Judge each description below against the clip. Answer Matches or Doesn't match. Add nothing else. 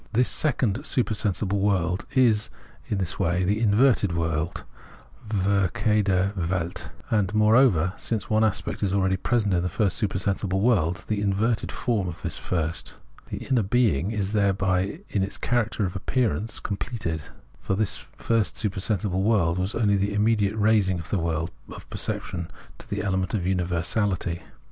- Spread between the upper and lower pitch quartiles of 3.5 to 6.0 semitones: Doesn't match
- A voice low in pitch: Matches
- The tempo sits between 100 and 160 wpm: Matches